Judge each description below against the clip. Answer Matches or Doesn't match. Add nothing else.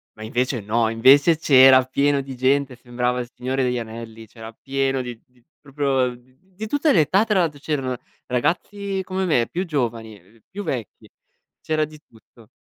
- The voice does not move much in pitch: Doesn't match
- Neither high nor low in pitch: Doesn't match